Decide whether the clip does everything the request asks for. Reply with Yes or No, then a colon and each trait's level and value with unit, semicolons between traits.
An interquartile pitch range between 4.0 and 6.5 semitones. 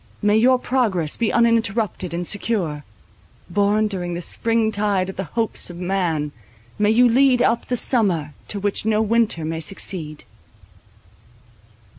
Yes: average, 4.6 semitones